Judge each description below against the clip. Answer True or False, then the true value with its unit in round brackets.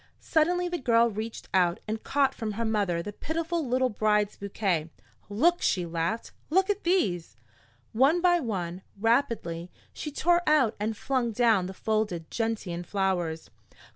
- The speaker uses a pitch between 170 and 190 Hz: False (220 Hz)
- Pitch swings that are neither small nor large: False (6.7 semitones)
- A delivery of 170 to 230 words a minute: False (150 wpm)